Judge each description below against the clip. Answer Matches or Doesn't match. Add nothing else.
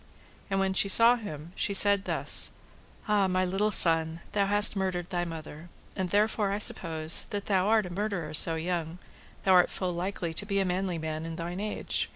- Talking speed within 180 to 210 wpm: Matches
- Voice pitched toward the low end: Doesn't match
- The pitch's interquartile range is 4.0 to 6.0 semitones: Doesn't match